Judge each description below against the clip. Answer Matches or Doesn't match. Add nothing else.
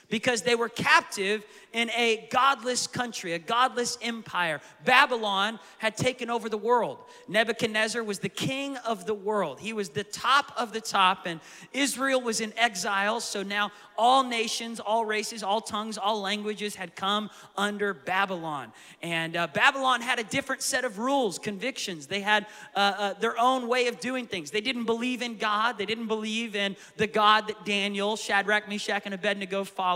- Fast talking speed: Doesn't match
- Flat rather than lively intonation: Doesn't match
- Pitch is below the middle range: Doesn't match